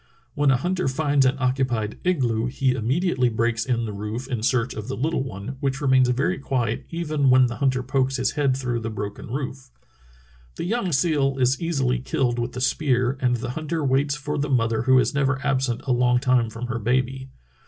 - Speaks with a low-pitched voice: Yes, low, 130 Hz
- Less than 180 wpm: No, fast, 205 wpm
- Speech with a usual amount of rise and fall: No, narrow, 2.3 semitones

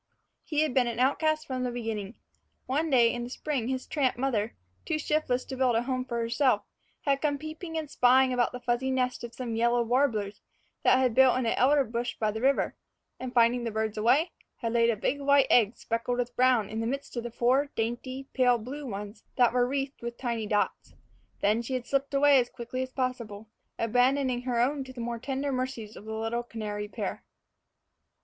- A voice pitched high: Yes, high, 245 Hz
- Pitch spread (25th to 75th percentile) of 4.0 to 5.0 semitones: No, narrow, 2.4 semitones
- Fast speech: Yes, fast, 210 wpm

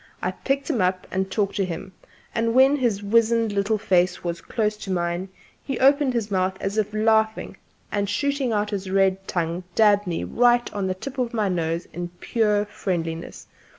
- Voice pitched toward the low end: No, high, 205 Hz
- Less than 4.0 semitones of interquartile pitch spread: Yes, average, 3.6 semitones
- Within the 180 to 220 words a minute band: Yes, average, 185 wpm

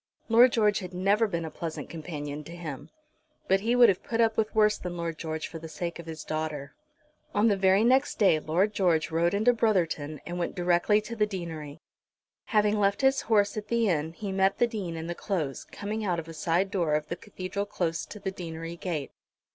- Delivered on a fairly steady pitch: No, average, 4.3 semitones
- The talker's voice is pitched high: No, medium, 180 Hz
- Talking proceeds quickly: Yes, fast, 220 wpm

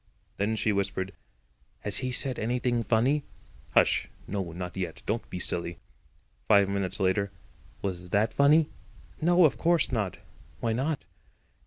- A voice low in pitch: Yes, low, 105 Hz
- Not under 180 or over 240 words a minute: No, average, 140 wpm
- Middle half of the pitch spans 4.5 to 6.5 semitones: Yes, average, 5.0 semitones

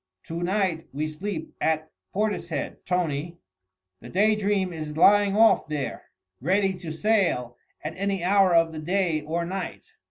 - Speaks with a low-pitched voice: No, medium, 175 Hz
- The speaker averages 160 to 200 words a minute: No, average, 150 wpm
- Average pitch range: Yes, average, 4.0 semitones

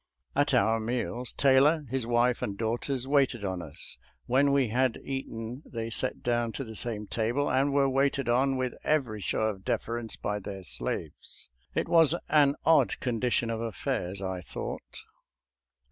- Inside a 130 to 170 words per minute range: Yes, average, 160 wpm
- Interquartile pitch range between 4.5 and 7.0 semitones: No, average, 3.5 semitones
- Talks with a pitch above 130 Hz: No, low, 120 Hz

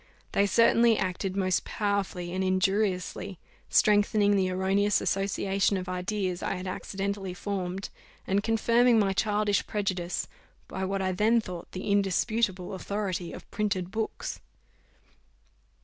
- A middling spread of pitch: No, narrow, 1.8 semitones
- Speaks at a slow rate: Yes, slow, 125 wpm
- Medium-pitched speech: No, high, 195 Hz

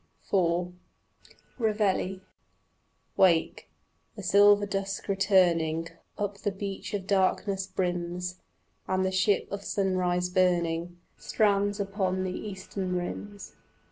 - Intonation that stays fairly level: Yes, narrow, 2.0 semitones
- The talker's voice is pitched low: No, high, 190 Hz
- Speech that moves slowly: Yes, slow, 105 wpm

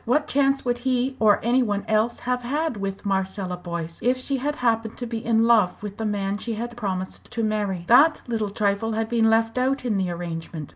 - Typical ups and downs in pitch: Yes, average, 3.7 semitones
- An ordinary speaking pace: No, fast, 220 wpm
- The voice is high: Yes, high, 225 Hz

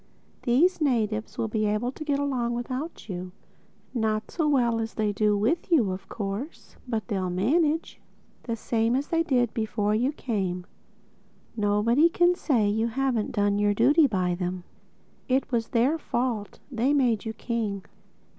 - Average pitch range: Yes, average, 4.5 semitones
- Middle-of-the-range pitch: No, high, 230 Hz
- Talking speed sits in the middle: Yes, average, 150 wpm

